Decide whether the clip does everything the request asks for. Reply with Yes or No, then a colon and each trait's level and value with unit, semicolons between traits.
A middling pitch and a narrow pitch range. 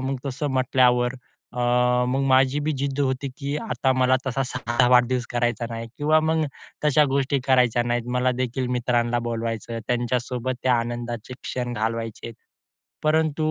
No: low, 125 Hz; narrow, 2.1 semitones